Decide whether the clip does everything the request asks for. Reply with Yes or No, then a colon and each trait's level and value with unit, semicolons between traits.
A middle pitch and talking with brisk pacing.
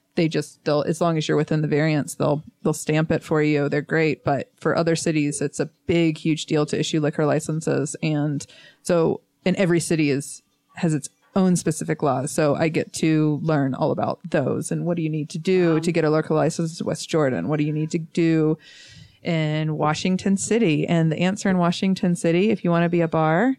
Yes: medium, 160 Hz; fast, 220 wpm